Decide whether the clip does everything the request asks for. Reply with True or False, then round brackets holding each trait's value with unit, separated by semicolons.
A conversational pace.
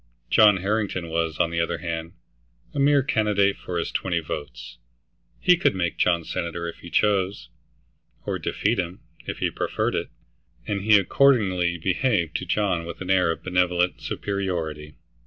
True (160 wpm)